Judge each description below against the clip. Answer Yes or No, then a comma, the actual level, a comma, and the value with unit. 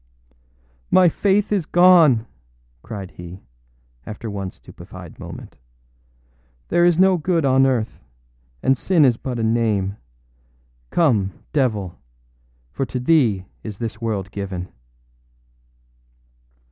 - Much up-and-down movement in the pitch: Yes, wide, 8.1 semitones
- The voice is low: Yes, low, 120 Hz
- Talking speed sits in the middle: No, slow, 110 wpm